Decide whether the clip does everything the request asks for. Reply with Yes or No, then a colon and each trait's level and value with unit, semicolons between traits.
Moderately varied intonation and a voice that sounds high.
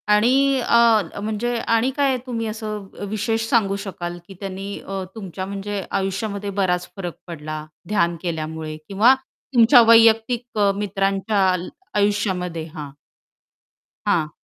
Yes: average, 3.4 semitones; high, 200 Hz